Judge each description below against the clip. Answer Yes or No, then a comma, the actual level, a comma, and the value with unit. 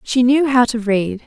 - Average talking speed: No, fast, 235 wpm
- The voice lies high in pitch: Yes, high, 240 Hz